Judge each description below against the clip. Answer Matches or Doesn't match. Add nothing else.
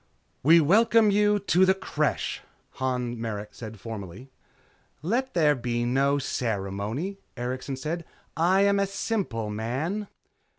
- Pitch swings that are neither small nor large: Doesn't match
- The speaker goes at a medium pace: Doesn't match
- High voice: Doesn't match